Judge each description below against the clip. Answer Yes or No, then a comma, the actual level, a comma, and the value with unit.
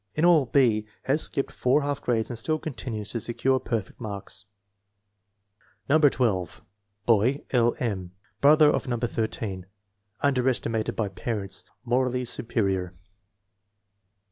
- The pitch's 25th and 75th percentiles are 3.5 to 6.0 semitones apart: Yes, average, 3.8 semitones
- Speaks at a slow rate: Yes, slow, 125 wpm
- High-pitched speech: No, low, 120 Hz